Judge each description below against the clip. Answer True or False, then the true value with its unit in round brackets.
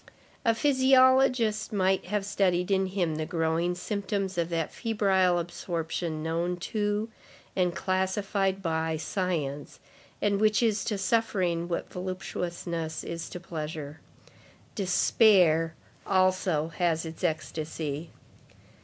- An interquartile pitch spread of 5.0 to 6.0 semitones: False (3.5 semitones)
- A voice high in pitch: False (180 Hz)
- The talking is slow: True (110 wpm)